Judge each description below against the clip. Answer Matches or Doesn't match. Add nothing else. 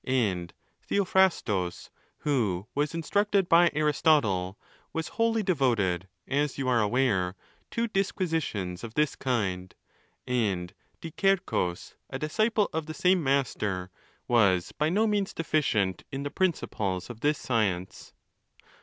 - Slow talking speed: Matches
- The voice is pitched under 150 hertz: Matches